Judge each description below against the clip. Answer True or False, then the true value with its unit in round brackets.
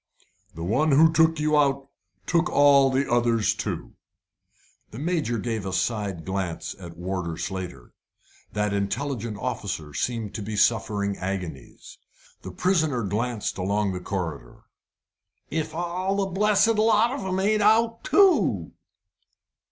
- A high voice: False (120 Hz)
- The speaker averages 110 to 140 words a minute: True (135 wpm)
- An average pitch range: False (9.0 semitones)